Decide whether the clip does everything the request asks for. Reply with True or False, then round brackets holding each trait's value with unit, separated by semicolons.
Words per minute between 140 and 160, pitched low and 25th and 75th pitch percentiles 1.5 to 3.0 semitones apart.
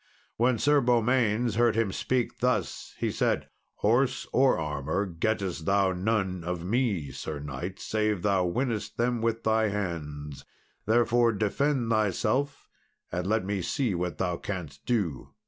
False (145 wpm; 105 Hz; 4.9 semitones)